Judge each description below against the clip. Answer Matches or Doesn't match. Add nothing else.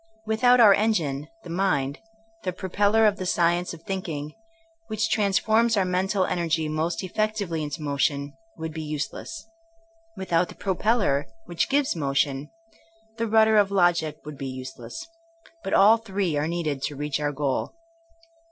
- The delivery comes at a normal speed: Matches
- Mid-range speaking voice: Matches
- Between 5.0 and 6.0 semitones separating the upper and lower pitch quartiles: Matches